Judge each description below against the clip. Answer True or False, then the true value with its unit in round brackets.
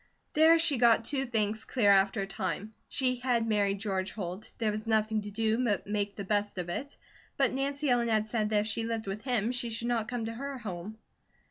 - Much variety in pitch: False (3.0 semitones)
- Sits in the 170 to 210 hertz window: False (220 Hz)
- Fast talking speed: True (225 wpm)